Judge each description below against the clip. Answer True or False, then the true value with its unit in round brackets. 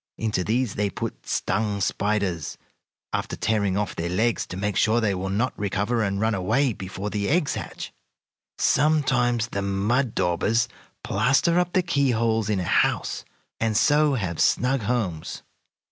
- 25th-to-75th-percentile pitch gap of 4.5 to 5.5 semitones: False (3.8 semitones)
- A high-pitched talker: False (110 Hz)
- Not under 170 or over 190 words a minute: False (155 wpm)